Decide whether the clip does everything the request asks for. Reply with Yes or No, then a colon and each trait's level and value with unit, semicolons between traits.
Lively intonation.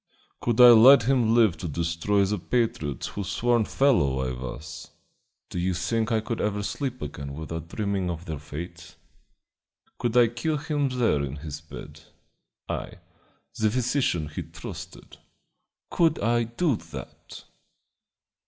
Yes: wide, 7.0 semitones